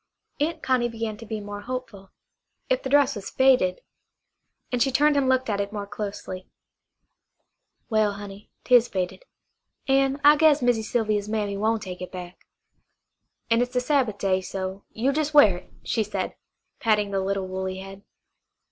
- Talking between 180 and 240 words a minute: No, average, 165 wpm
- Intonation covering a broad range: No, average, 4.6 semitones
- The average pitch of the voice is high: Yes, high, 215 Hz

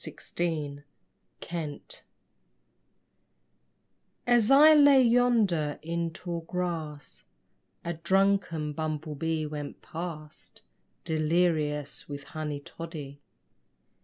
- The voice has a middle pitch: Yes, medium, 165 Hz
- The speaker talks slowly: Yes, slow, 80 wpm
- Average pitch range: Yes, average, 3.1 semitones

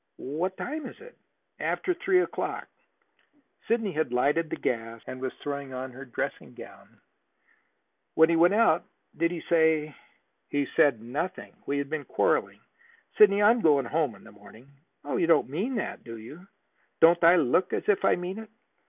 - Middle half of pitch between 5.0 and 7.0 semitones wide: Yes, wide, 5.6 semitones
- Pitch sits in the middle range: Yes, medium, 160 Hz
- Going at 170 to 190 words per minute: Yes, average, 180 wpm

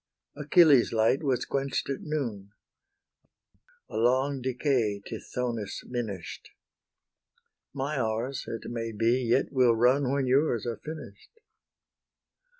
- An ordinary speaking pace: No, slow, 110 wpm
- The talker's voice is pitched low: Yes, low, 125 Hz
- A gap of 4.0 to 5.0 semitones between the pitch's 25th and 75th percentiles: No, average, 3.2 semitones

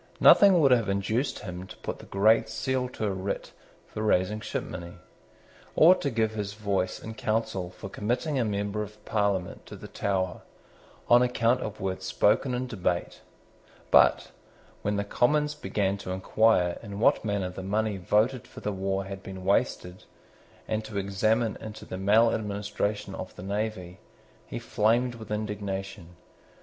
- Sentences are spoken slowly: No, average, 160 wpm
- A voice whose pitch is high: No, low, 105 Hz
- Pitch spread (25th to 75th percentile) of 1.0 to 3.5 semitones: Yes, narrow, 2.6 semitones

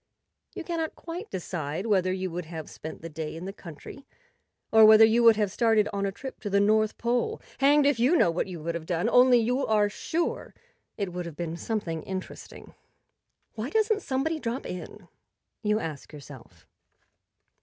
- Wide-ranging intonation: Yes, wide, 6.1 semitones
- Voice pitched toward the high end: Yes, high, 210 Hz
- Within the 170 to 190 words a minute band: Yes, average, 185 wpm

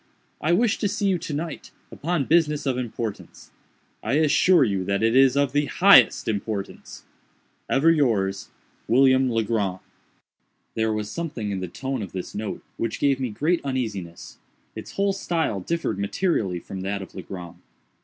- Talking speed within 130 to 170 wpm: Yes, average, 160 wpm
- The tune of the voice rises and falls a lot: Yes, wide, 7.4 semitones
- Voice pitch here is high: No, low, 125 Hz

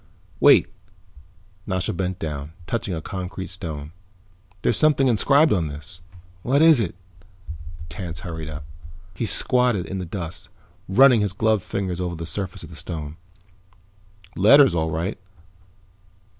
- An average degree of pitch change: Yes, average, 5.0 semitones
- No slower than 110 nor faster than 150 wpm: Yes, slow, 135 wpm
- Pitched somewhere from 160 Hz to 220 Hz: No, very low, 90 Hz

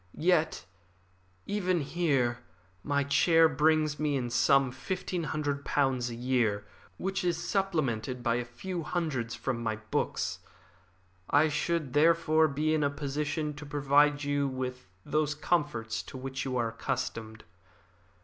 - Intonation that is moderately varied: Yes, average, 3.7 semitones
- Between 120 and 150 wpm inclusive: Yes, average, 140 wpm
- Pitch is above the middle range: No, medium, 145 Hz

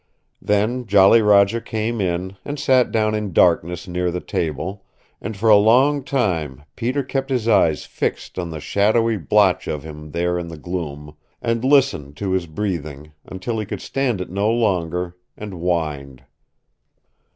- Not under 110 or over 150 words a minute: No, average, 165 wpm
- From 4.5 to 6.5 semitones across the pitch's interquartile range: Yes, average, 5.2 semitones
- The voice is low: Yes, very low, 95 Hz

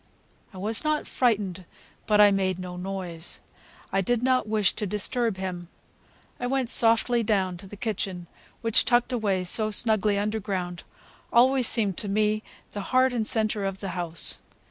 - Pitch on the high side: Yes, high, 210 Hz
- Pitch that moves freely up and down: No, average, 3.4 semitones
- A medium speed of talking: Yes, average, 165 wpm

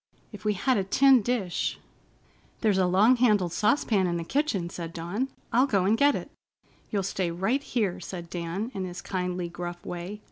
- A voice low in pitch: No, high, 195 Hz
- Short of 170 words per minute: No, average, 185 wpm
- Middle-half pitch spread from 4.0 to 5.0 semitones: Yes, average, 4.4 semitones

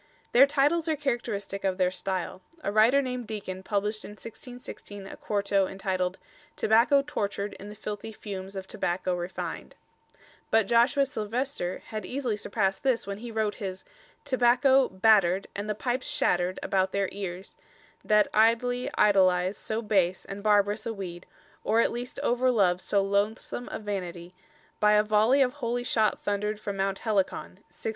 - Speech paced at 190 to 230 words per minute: No, average, 160 wpm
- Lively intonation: No, average, 3.6 semitones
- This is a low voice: No, high, 210 Hz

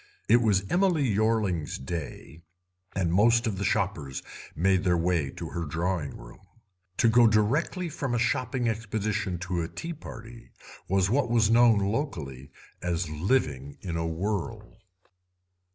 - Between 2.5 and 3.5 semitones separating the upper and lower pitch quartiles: No, average, 5.3 semitones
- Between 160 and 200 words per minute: No, average, 145 wpm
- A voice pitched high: No, low, 100 Hz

